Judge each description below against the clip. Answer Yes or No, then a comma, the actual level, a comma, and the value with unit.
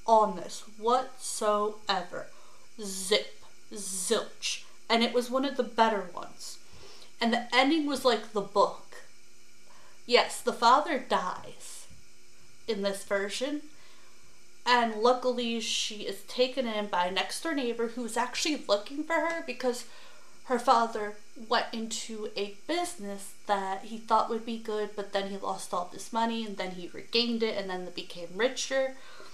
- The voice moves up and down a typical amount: Yes, average, 3.5 semitones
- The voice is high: Yes, high, 230 Hz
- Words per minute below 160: Yes, average, 150 wpm